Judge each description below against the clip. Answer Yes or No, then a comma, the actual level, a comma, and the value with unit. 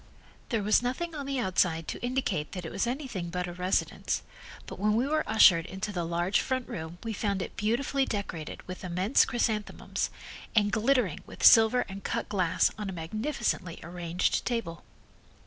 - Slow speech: No, average, 175 wpm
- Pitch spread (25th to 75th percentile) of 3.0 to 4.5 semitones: No, average, 5.3 semitones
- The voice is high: Yes, high, 205 Hz